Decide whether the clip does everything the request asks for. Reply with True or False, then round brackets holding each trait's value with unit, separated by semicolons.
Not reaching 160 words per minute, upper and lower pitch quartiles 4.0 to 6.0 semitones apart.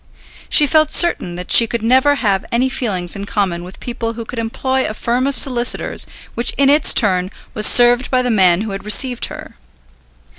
False (195 wpm; 4.4 semitones)